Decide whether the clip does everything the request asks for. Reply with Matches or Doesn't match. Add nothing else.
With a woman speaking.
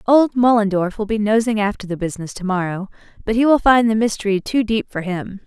Matches